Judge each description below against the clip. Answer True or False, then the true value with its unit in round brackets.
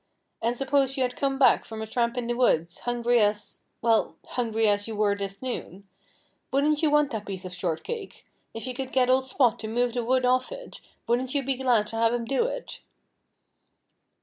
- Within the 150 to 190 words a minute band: False (205 wpm)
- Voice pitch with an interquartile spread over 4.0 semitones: False (3.2 semitones)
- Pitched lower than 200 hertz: False (240 Hz)